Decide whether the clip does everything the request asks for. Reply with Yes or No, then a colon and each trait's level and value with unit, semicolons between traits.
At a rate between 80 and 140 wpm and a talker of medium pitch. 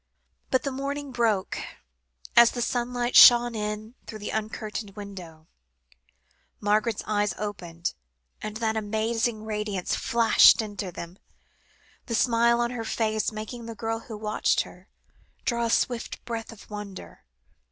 No: slow, 135 wpm; high, 220 Hz